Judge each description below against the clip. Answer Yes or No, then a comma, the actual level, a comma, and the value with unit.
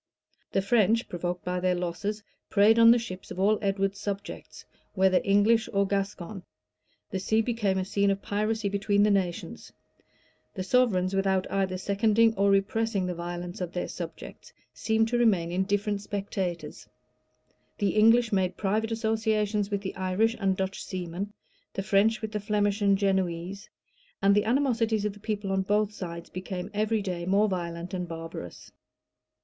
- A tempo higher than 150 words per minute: Yes, average, 160 wpm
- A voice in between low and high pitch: No, high, 200 Hz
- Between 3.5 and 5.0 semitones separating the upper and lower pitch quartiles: No, narrow, 2.4 semitones